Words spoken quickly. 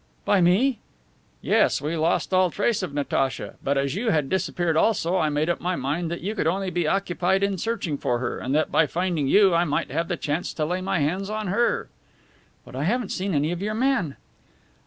Yes: fast, 220 wpm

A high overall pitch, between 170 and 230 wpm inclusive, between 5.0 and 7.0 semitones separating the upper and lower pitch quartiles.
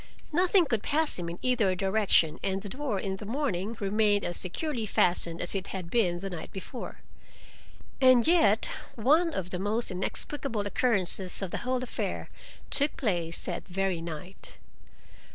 No: high, 205 Hz; average, 160 wpm; wide, 5.5 semitones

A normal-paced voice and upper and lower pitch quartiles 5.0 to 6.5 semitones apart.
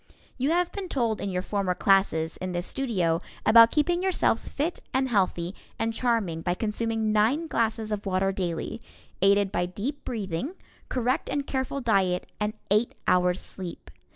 Yes: average, 160 wpm; wide, 5.5 semitones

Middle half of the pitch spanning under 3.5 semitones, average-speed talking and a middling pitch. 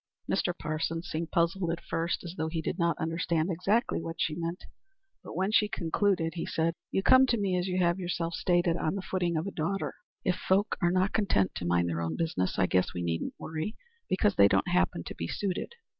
No: average, 2.9 semitones; fast, 220 wpm; medium, 170 Hz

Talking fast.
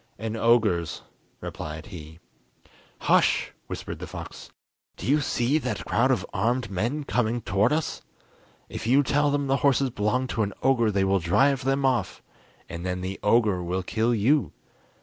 No: average, 165 wpm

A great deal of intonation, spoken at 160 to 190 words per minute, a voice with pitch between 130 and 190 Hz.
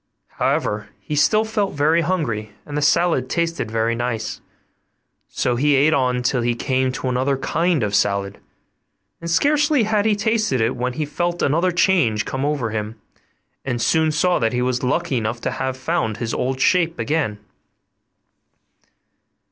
Yes: wide, 6.0 semitones; average, 165 wpm; low, 135 Hz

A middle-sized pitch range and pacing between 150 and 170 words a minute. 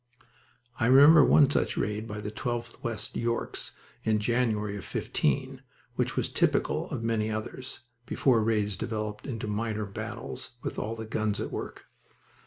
No: narrow, 1.8 semitones; average, 155 wpm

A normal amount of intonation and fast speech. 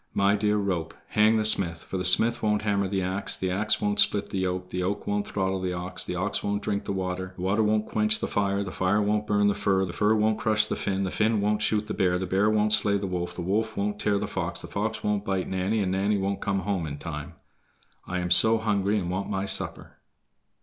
No: narrow, 2.2 semitones; fast, 255 wpm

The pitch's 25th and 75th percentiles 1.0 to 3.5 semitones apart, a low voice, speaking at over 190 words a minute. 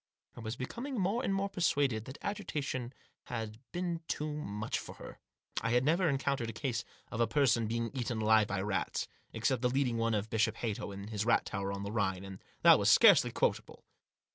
No: average, 5.0 semitones; low, 115 Hz; average, 200 wpm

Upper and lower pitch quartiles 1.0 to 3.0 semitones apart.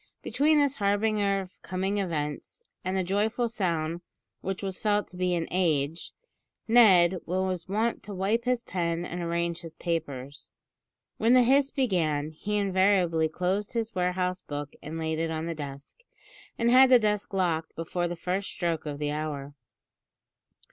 No: average, 4.1 semitones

